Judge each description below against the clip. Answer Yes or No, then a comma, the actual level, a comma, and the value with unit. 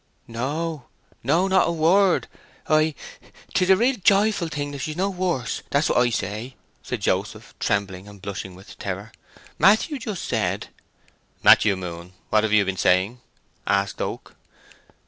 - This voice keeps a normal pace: Yes, average, 145 wpm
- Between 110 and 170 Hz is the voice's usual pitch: Yes, low, 135 Hz